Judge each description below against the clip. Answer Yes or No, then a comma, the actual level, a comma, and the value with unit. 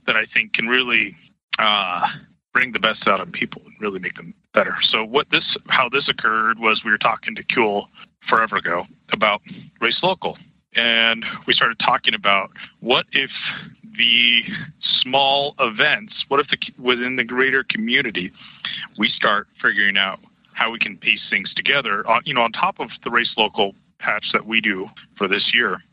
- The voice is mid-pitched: No, low, 125 Hz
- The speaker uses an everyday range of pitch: Yes, average, 3.3 semitones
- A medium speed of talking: Yes, average, 175 wpm